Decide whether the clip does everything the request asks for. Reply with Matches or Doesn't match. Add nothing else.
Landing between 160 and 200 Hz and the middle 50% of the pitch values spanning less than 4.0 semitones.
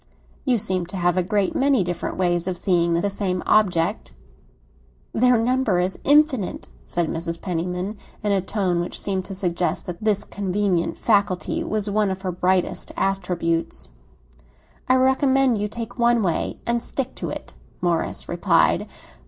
Matches